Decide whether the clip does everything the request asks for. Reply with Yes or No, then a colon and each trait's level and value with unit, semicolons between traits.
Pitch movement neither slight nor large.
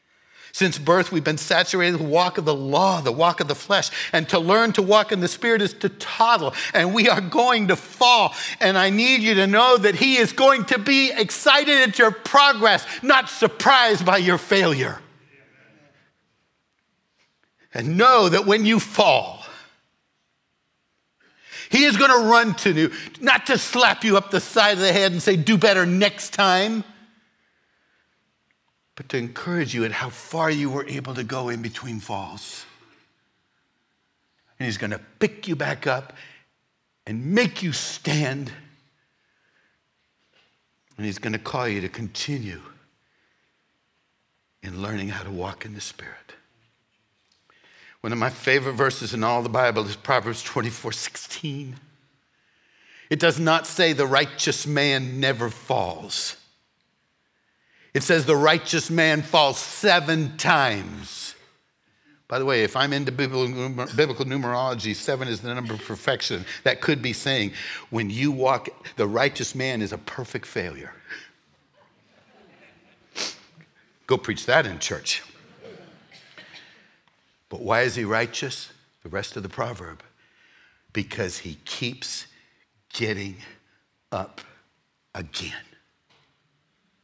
No: wide, 8.5 semitones